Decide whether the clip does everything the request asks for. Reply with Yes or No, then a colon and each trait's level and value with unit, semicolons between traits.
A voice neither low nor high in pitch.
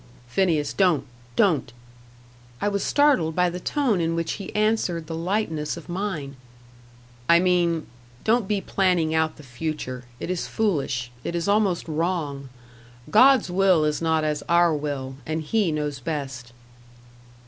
Yes: medium, 165 Hz